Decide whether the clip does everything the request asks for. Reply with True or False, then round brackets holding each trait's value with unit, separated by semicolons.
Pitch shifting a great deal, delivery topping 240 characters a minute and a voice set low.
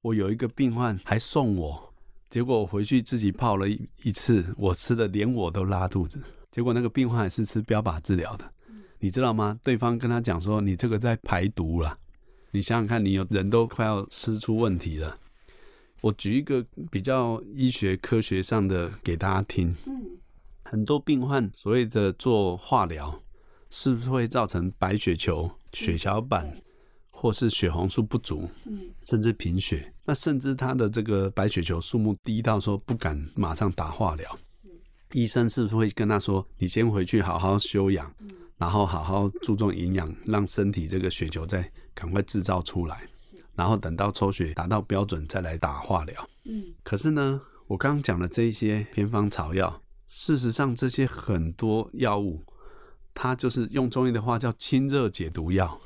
False (4.2 semitones; 255 characters per minute; 105 Hz)